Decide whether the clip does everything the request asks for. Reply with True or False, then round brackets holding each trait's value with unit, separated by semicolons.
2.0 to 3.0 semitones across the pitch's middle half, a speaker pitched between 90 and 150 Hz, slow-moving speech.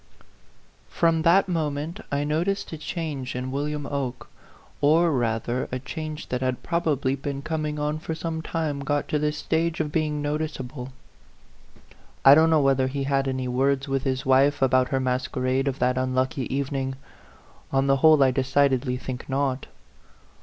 False (2.7 semitones; 140 Hz; 165 wpm)